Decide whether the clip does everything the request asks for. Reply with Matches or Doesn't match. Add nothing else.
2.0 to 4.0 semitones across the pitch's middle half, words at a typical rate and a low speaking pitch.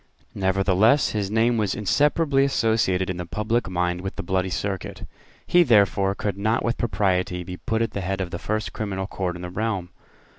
Matches